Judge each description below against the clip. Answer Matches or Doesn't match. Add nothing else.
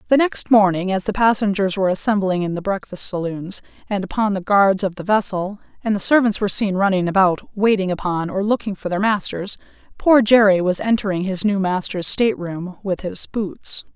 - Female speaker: Matches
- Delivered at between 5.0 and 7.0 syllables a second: Matches